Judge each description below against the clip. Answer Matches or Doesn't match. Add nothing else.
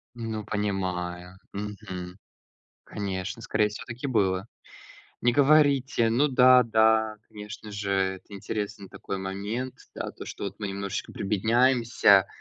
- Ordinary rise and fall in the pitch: Matches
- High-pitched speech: Doesn't match